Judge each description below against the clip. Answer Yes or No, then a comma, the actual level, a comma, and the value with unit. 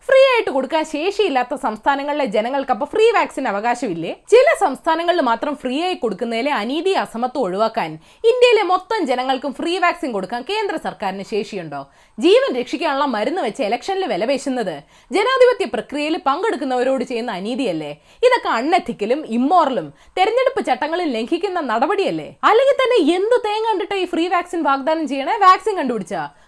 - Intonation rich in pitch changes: Yes, wide, 8.0 semitones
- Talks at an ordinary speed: No, fast, 130 wpm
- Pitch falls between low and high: No, very high, 295 Hz